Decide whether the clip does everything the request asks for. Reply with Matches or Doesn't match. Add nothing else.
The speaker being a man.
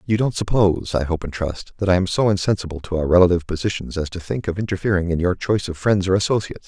Matches